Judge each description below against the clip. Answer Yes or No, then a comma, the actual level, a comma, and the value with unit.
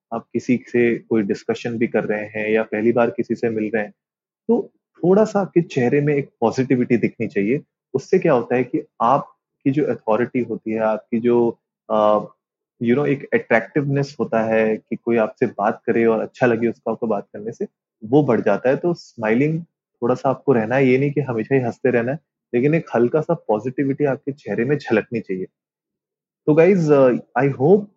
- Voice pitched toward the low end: Yes, low, 120 Hz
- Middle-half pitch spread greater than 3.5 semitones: Yes, average, 4.0 semitones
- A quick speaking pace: Yes, fast, 200 wpm